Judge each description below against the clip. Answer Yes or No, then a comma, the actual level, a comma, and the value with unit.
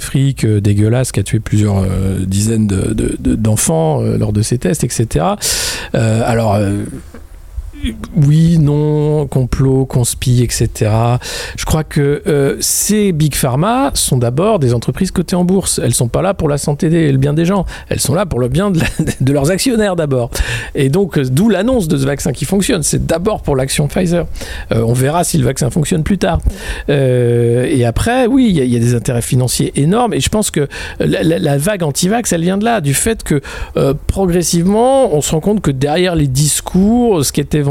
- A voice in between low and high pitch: Yes, medium, 145 Hz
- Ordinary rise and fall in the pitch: No, wide, 6.7 semitones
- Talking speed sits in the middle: Yes, average, 210 wpm